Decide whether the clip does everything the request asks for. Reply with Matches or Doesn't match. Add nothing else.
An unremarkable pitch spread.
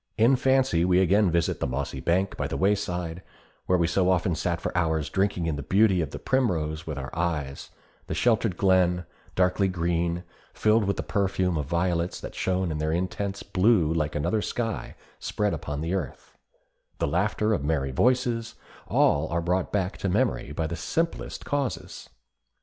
Matches